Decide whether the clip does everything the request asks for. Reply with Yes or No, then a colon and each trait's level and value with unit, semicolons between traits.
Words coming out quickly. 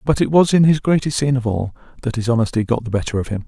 Yes: fast, 295 wpm